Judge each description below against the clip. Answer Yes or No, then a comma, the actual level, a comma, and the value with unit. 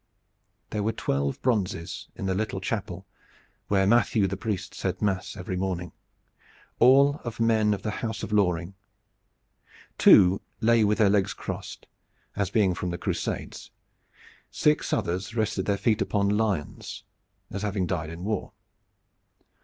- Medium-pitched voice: No, low, 100 Hz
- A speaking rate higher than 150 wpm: No, average, 145 wpm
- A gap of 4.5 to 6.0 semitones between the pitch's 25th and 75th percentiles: No, average, 3.0 semitones